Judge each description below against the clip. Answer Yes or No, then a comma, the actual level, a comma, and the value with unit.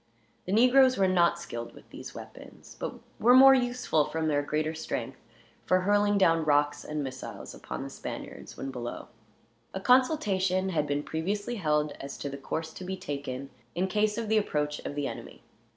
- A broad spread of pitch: Yes, wide, 5.8 semitones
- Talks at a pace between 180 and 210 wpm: Yes, average, 185 wpm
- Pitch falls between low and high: Yes, medium, 170 Hz